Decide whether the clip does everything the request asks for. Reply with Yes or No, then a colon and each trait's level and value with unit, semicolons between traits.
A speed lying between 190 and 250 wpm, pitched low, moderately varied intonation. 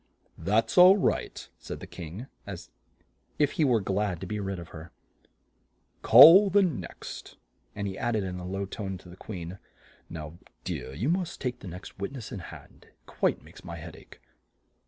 No: average, 195 wpm; low, 100 Hz; wide, 5.8 semitones